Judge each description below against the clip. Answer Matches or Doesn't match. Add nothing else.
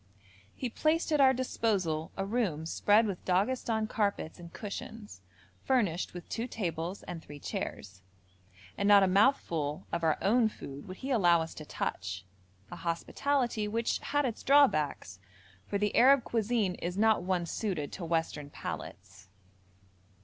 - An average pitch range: Doesn't match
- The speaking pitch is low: Doesn't match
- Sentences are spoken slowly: Doesn't match